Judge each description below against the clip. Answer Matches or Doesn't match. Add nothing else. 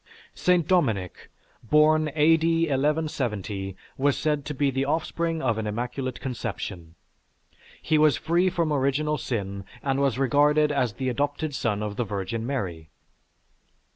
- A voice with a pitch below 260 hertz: Matches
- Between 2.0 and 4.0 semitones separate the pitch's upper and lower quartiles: Doesn't match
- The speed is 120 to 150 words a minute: Matches